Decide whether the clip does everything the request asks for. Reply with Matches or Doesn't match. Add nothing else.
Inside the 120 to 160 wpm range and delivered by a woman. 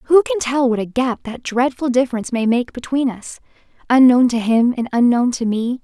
Doesn't match